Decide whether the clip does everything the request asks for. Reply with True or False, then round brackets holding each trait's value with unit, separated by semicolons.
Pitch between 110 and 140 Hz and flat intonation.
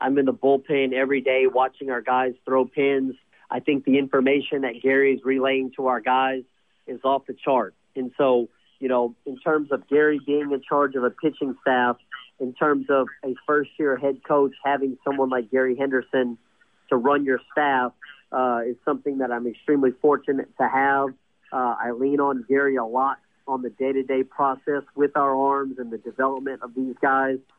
True (135 Hz; 1.4 semitones)